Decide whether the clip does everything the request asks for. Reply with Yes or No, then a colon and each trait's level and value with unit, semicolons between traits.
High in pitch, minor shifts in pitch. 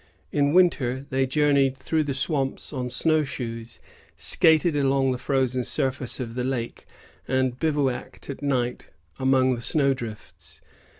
No: low, 135 Hz; narrow, 2.2 semitones